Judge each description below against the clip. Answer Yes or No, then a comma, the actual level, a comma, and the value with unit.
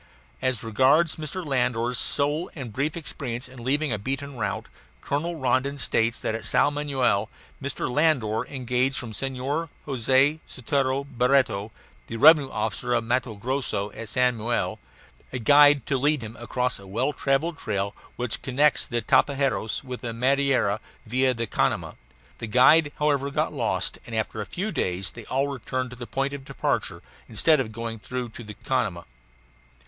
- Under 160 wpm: No, average, 165 wpm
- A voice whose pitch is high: No, low, 130 Hz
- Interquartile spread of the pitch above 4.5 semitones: No, average, 3.5 semitones